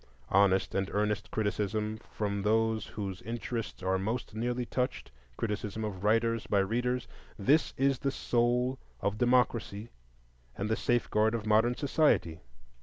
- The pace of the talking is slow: Yes, slow, 125 wpm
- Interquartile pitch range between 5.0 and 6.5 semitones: No, average, 2.9 semitones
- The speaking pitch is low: Yes, low, 110 Hz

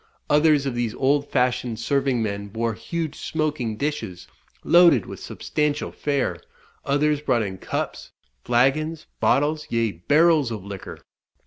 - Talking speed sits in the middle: No, slow, 130 wpm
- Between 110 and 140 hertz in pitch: Yes, low, 135 Hz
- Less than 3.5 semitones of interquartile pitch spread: No, average, 4.8 semitones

